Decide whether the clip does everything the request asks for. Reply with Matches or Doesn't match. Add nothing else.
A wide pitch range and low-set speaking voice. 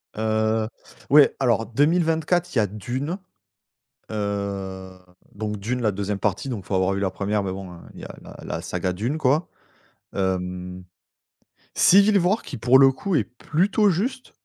Matches